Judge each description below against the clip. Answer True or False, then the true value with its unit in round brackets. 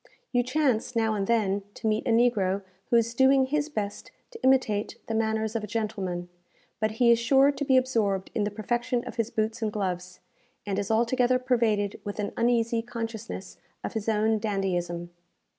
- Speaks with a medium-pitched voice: False (225 Hz)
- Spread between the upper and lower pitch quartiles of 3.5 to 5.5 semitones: False (2.8 semitones)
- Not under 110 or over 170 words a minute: False (185 wpm)